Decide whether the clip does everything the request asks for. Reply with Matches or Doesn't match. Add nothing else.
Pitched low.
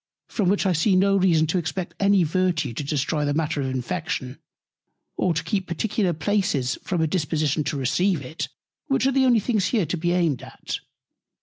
Doesn't match